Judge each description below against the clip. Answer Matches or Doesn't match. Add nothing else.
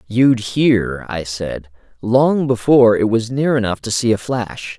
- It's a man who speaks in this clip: Matches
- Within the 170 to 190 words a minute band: Matches